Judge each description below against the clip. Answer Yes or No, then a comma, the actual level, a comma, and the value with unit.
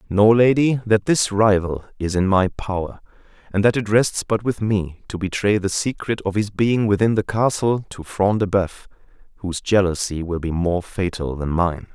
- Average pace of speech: Yes, average, 190 wpm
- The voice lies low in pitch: Yes, low, 100 Hz